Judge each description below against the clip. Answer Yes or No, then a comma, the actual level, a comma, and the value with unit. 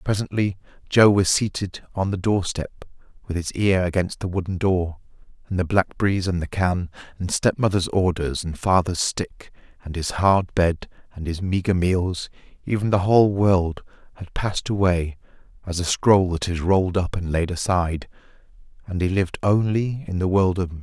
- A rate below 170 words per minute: No, average, 175 wpm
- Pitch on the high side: No, very low, 95 Hz